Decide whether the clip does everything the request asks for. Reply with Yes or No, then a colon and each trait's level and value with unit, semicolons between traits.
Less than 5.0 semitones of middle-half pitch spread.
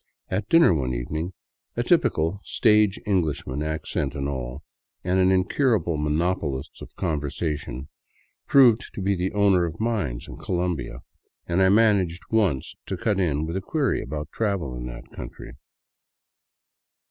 No: average, 5.3 semitones